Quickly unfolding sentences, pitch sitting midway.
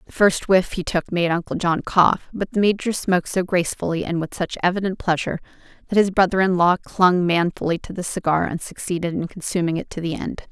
Yes: fast, 215 wpm; medium, 180 Hz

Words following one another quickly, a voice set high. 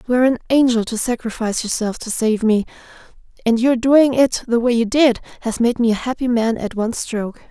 Yes: fast, 215 wpm; high, 235 Hz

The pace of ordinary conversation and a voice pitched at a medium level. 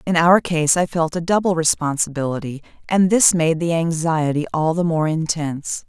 Yes: average, 175 wpm; medium, 165 Hz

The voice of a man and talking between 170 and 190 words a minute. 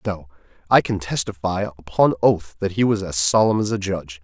No: male; average, 200 wpm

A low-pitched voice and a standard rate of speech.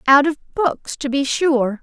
No: very high, 280 Hz; average, 195 wpm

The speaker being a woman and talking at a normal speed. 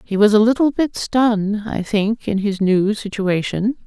Yes: female; average, 185 wpm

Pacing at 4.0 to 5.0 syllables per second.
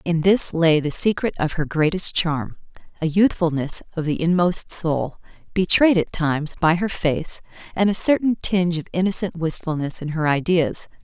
Yes: 4.8 syllables/s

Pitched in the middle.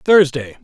Yes: medium, 150 Hz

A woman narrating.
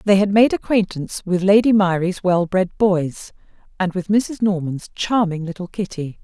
Yes: female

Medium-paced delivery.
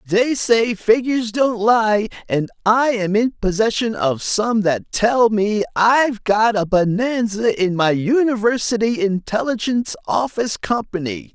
No: slow, 130 wpm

